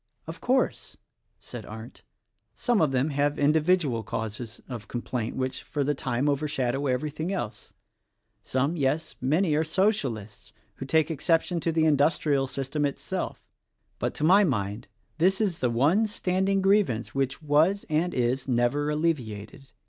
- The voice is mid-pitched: Yes, medium, 145 Hz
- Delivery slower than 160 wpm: Yes, average, 150 wpm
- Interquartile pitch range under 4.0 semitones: No, average, 4.4 semitones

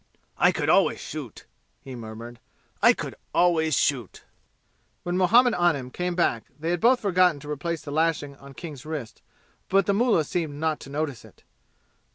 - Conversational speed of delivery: Yes, average, 170 wpm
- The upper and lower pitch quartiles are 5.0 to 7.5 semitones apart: No, average, 4.3 semitones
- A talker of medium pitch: Yes, medium, 160 Hz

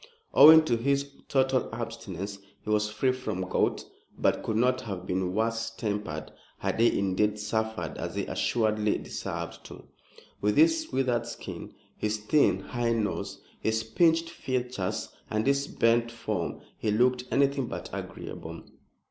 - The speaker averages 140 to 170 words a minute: Yes, average, 145 wpm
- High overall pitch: No, low, 115 Hz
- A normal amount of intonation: Yes, average, 3.5 semitones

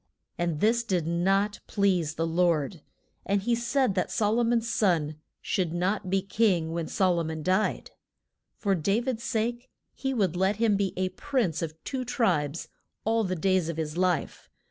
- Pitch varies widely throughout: No, average, 4.7 semitones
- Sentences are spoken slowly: No, average, 180 wpm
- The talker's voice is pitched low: No, high, 190 Hz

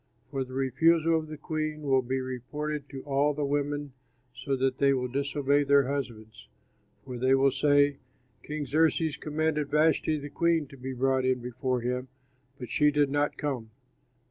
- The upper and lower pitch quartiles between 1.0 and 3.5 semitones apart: Yes, narrow, 2.4 semitones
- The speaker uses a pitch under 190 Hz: Yes, medium, 140 Hz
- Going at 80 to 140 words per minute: No, average, 170 wpm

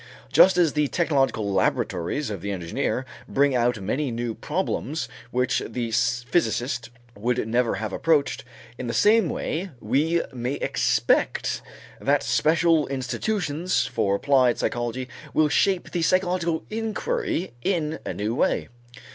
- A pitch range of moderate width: No, wide, 5.8 semitones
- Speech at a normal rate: No, slow, 130 wpm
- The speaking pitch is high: No, low, 135 Hz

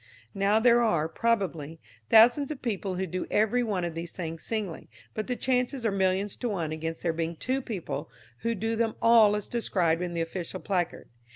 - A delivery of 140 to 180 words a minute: No, average, 195 wpm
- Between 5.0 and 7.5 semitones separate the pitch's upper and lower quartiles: Yes, average, 5.3 semitones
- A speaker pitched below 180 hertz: No, high, 200 Hz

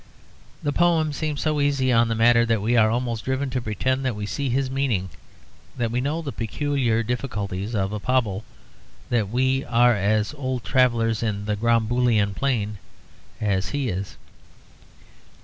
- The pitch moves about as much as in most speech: Yes, average, 3.7 semitones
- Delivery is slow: No, average, 165 wpm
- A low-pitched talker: Yes, low, 120 Hz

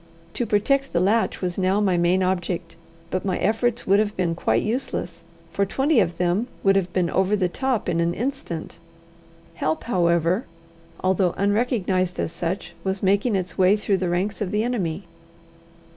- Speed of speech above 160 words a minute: Yes, average, 175 wpm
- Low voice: No, high, 190 Hz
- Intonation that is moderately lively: Yes, average, 3.2 semitones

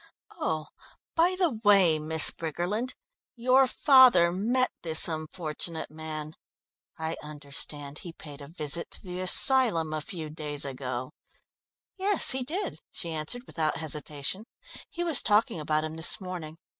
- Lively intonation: Yes, wide, 6.7 semitones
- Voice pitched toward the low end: No, medium, 165 Hz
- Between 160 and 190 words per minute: No, average, 140 wpm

